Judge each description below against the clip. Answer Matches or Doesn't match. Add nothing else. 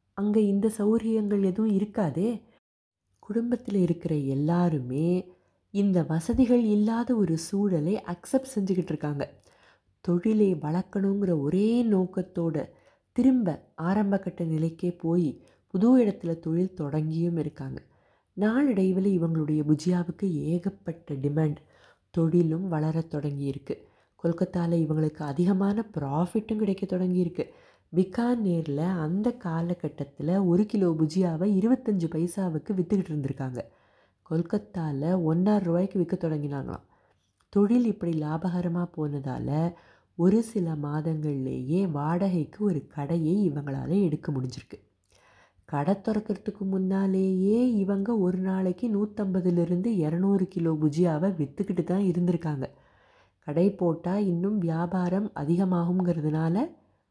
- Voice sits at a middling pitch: Matches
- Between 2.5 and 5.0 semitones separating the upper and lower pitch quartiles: Matches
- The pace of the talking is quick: Doesn't match